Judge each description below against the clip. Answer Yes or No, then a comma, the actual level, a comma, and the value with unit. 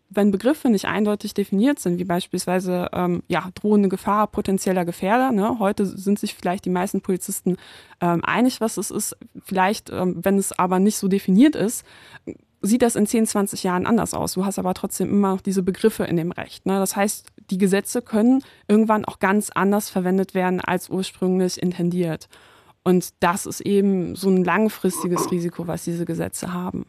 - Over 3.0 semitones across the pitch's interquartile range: No, narrow, 2.4 semitones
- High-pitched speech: Yes, high, 195 Hz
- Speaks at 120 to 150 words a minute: No, average, 185 wpm